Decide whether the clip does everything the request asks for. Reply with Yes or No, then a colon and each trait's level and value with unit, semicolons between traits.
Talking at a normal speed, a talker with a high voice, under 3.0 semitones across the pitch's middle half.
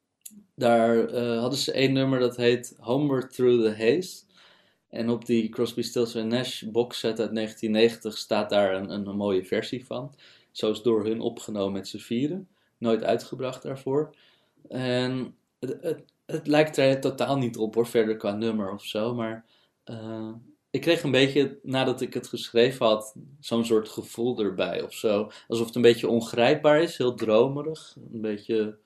No: average, 170 wpm; low, 120 Hz; narrow, 2.5 semitones